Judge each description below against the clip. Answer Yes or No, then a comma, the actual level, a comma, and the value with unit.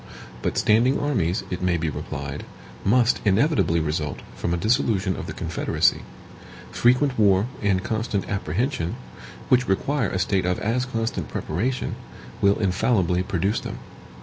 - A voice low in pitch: Yes, low, 100 Hz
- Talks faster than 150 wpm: No, average, 140 wpm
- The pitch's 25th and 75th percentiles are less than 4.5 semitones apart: No, average, 5.1 semitones